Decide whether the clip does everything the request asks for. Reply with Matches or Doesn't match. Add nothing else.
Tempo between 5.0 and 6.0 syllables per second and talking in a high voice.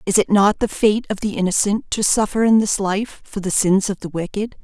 Matches